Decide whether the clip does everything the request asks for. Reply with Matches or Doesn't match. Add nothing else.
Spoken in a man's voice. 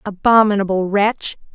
Doesn't match